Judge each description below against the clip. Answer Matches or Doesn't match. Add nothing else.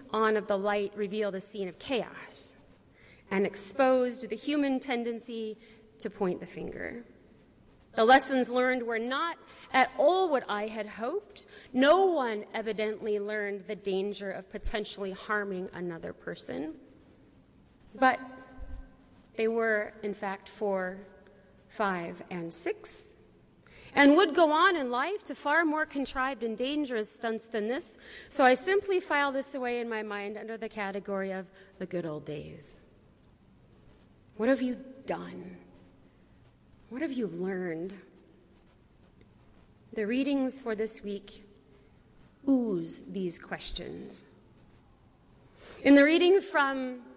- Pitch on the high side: Matches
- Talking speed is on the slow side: Matches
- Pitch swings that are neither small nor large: Matches